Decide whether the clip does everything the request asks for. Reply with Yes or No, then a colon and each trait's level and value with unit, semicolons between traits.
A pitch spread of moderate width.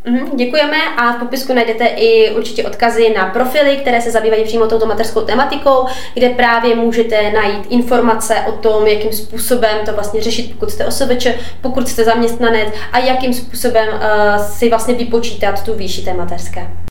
No: narrow, 2.2 semitones